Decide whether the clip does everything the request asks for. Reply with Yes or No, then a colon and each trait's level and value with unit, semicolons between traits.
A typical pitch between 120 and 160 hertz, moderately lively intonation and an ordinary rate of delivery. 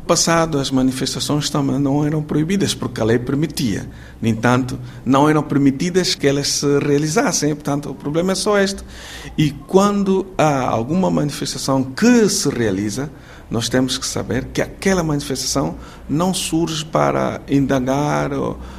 Yes: medium, 140 Hz; average, 3.6 semitones; average, 145 wpm